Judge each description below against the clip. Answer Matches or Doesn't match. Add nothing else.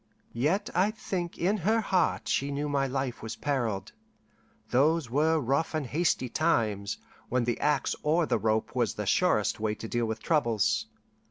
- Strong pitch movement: Matches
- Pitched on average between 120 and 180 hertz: Matches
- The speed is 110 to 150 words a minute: Doesn't match